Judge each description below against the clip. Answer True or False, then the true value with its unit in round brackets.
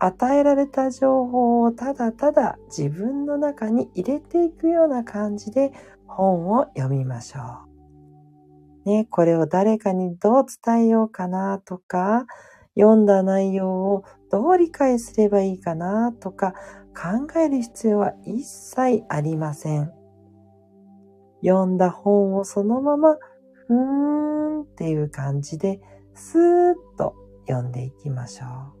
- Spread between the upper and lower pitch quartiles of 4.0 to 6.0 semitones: False (8.8 semitones)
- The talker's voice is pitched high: True (200 Hz)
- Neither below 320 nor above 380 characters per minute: False (245 characters per minute)